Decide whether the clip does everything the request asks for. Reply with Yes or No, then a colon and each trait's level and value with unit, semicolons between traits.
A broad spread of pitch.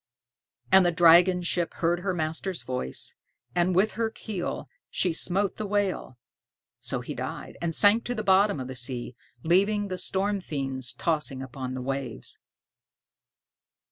Yes: wide, 6.3 semitones